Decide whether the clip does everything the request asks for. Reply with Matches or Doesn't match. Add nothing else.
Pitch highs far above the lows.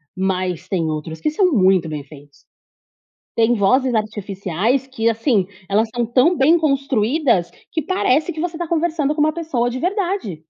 Matches